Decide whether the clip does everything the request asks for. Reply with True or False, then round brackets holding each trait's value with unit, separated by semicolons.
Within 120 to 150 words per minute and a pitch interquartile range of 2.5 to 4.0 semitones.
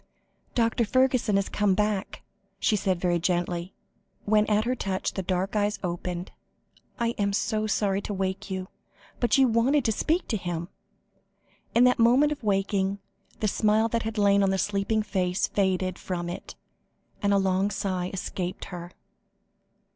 False (160 wpm; 2.8 semitones)